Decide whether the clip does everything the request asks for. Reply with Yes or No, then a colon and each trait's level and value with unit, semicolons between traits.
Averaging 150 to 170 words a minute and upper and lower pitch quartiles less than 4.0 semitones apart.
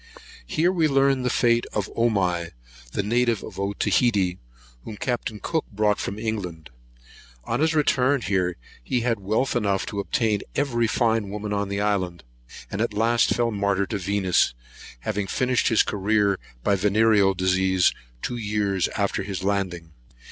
Yes: average, 160 wpm; average, 3.3 semitones